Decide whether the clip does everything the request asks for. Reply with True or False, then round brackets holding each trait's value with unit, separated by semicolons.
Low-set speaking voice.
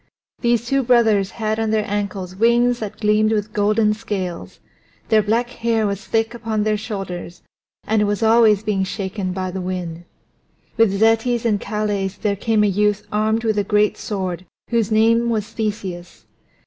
False (210 Hz)